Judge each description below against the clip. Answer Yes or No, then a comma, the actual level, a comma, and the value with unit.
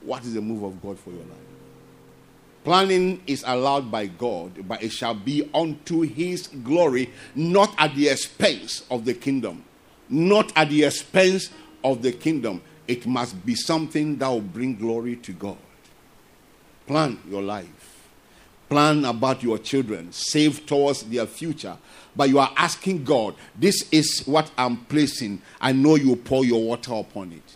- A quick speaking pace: No, average, 160 wpm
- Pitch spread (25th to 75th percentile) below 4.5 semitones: No, average, 5.1 semitones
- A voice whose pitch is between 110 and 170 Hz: Yes, low, 135 Hz